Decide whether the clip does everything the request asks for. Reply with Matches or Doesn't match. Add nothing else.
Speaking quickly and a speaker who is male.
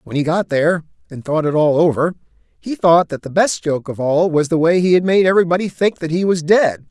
Matches